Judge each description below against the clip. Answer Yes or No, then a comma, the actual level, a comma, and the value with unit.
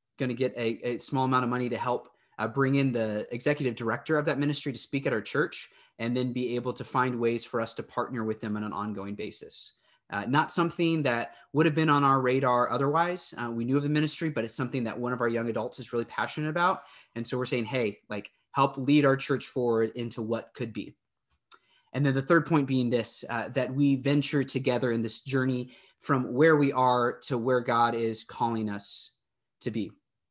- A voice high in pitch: No, low, 125 Hz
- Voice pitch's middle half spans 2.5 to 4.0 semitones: Yes, average, 3.1 semitones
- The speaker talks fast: Yes, fast, 225 wpm